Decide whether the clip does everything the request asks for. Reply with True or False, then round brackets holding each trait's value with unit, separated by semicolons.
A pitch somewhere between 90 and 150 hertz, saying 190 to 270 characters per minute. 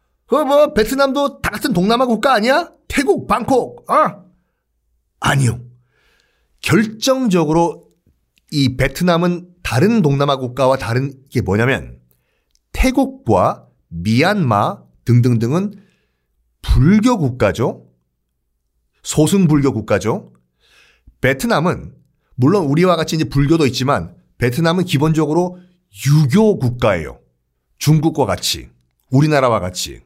True (140 Hz; 235 characters per minute)